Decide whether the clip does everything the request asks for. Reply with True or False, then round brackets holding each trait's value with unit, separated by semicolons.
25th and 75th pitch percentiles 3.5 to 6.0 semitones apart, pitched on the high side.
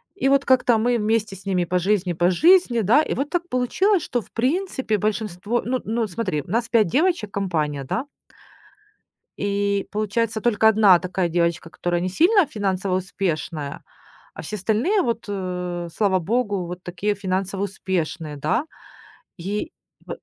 True (4.7 semitones; 205 Hz)